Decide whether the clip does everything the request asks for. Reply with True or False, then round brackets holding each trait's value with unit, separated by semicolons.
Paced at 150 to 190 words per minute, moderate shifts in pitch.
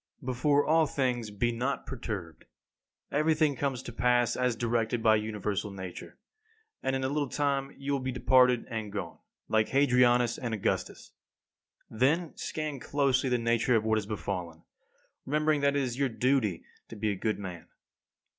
True (165 wpm; 4.0 semitones)